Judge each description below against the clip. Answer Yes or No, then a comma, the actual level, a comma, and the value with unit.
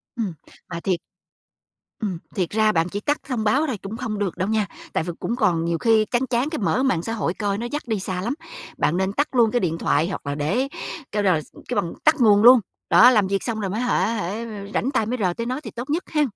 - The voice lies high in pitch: Yes, high, 215 Hz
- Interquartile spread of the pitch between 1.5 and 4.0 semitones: No, average, 4.6 semitones